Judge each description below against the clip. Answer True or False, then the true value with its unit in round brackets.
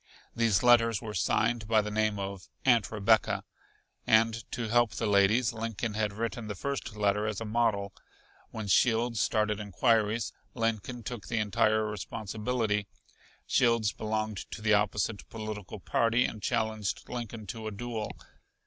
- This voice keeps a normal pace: True (150 wpm)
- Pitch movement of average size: False (1.7 semitones)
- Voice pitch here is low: True (110 Hz)